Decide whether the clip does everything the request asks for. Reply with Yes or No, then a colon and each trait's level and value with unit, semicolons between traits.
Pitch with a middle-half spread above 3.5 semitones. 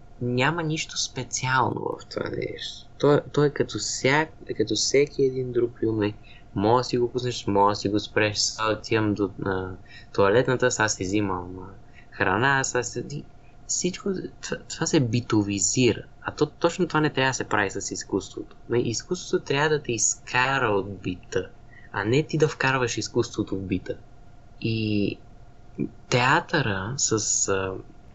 Yes: average, 4.4 semitones